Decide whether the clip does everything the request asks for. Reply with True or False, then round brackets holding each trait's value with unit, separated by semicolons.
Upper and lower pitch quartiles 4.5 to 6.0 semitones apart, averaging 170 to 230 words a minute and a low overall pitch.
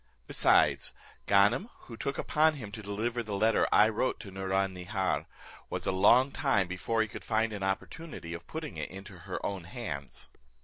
False (3.8 semitones; 180 wpm; 105 Hz)